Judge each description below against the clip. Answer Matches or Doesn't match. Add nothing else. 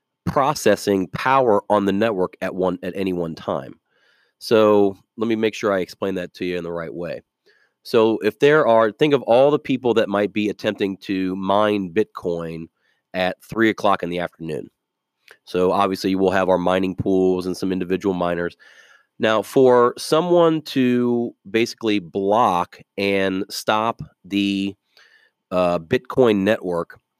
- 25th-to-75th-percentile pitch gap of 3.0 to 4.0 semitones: Matches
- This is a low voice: Matches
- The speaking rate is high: Doesn't match